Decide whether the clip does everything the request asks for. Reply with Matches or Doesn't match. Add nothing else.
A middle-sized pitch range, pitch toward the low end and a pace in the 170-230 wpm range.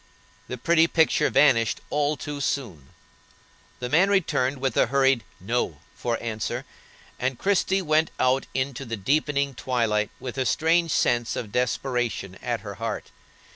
Doesn't match